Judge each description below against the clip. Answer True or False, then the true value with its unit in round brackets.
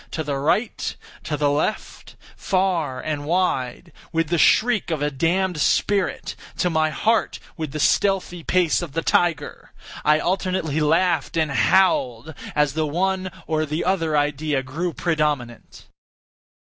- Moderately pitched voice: True (160 Hz)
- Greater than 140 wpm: False (135 wpm)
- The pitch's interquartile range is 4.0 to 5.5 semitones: False (3.5 semitones)